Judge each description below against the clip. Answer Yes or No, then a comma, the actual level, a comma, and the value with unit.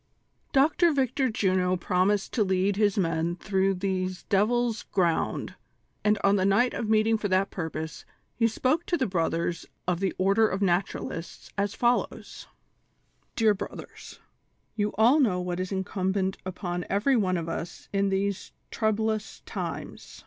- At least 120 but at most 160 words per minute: Yes, average, 155 wpm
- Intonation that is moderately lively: Yes, average, 3.0 semitones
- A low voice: No, high, 195 Hz